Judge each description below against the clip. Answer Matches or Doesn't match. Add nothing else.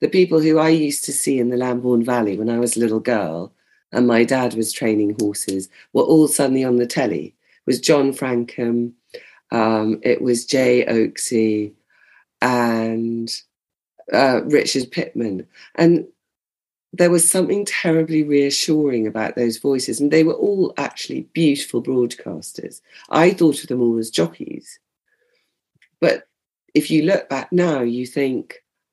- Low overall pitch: Matches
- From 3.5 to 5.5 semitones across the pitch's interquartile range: Matches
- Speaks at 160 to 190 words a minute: Doesn't match